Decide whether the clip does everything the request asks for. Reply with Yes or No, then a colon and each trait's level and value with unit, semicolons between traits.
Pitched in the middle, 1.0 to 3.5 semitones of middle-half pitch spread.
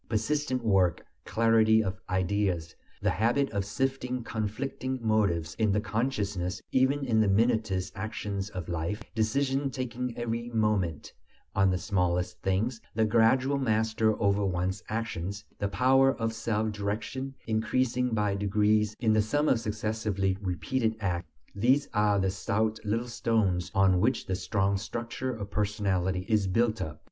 No: low, 110 Hz; average, 3.2 semitones